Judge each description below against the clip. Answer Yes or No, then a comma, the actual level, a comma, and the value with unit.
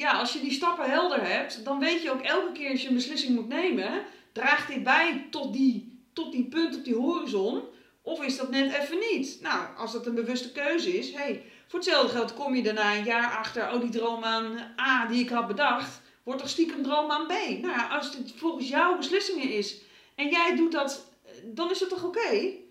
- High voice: Yes, very high, 280 Hz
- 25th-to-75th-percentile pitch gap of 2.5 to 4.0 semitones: No, average, 5.1 semitones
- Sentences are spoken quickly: Yes, fast, 230 wpm